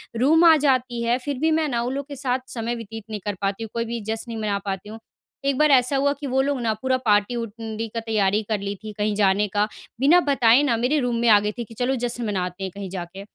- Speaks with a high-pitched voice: Yes, high, 230 Hz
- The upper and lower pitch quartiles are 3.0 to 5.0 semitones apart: Yes, average, 3.8 semitones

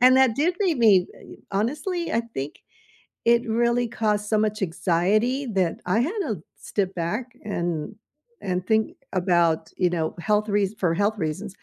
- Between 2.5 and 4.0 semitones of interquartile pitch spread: No, average, 4.7 semitones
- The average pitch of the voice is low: No, high, 210 Hz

